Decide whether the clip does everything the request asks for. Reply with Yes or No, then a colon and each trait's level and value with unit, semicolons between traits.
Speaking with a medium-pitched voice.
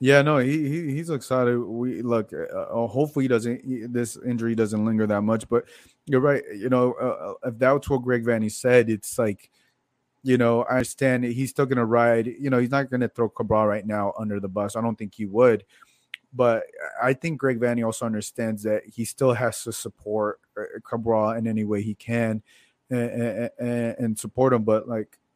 No: low, 120 Hz